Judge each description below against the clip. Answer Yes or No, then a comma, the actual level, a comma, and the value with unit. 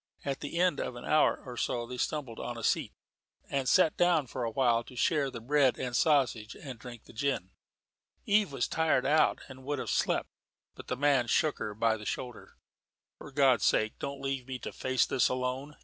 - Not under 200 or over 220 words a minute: Yes, fast, 205 wpm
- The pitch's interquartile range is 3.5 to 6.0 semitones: No, average, 3.0 semitones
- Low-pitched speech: Yes, low, 130 Hz